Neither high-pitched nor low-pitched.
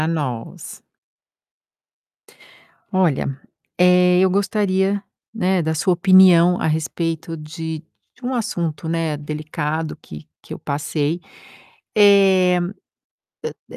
Yes: medium, 170 Hz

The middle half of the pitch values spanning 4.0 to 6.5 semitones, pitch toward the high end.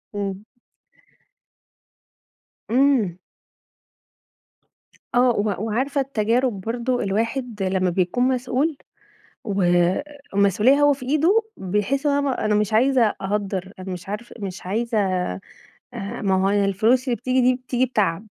Yes: average, 4.7 semitones; high, 220 Hz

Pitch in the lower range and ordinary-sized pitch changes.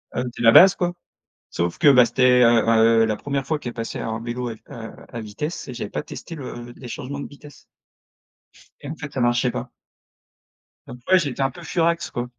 Yes: low, 125 Hz; average, 3.5 semitones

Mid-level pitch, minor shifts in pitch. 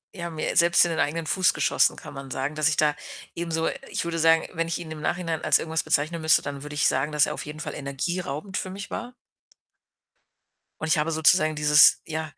Yes: medium, 160 Hz; narrow, 2.1 semitones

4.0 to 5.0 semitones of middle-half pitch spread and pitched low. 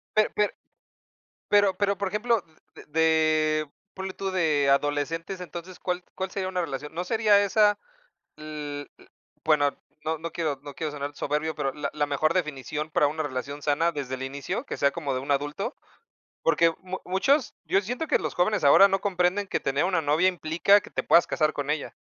No: average, 4.4 semitones; medium, 160 Hz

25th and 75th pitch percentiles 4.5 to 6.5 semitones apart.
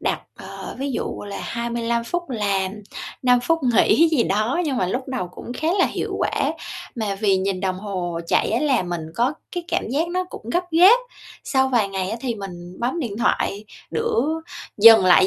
Yes: wide, 5.6 semitones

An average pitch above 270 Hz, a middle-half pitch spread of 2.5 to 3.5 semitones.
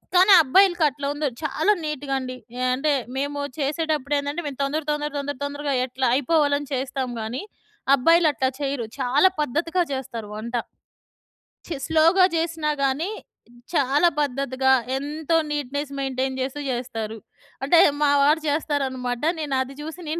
Yes: very high, 285 Hz; average, 2.8 semitones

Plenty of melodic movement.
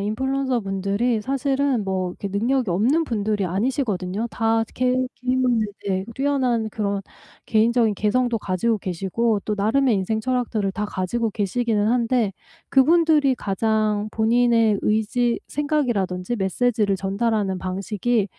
No: average, 3.8 semitones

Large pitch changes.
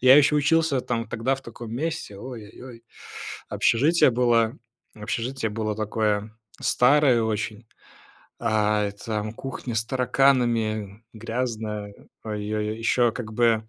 No: average, 2.8 semitones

